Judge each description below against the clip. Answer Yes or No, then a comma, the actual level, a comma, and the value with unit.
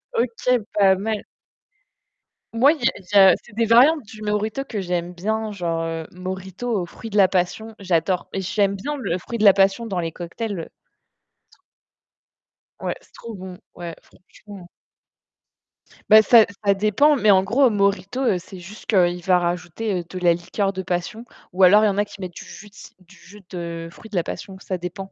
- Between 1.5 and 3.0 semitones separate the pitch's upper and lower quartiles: No, average, 3.4 semitones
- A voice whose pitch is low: No, high, 195 Hz